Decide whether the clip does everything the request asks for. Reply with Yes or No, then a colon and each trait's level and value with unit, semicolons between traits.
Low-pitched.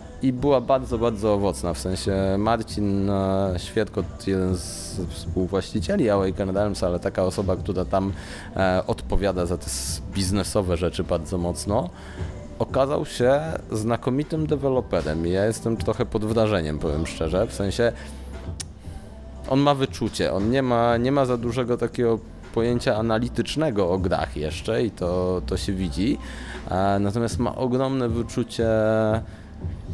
Yes: low, 100 Hz